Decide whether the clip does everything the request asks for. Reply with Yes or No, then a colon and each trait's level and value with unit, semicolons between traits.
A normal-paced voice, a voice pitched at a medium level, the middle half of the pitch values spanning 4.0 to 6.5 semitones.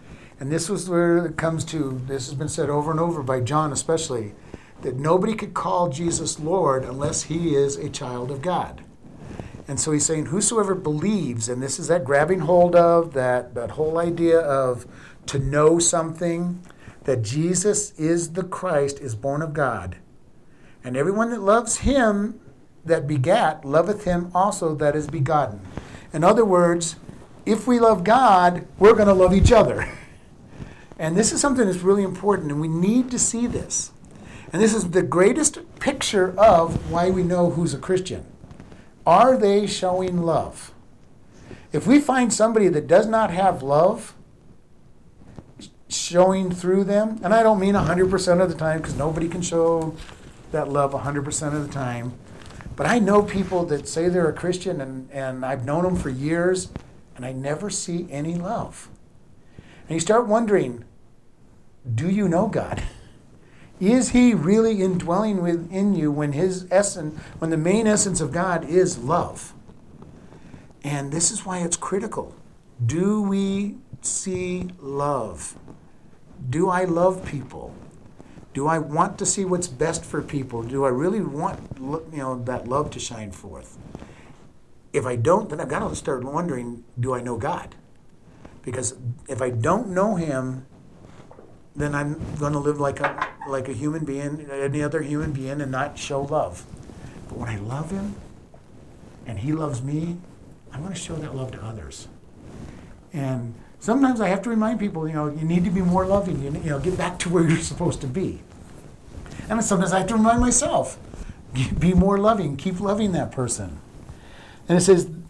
Yes: average, 170 wpm; medium, 165 Hz; average, 5.1 semitones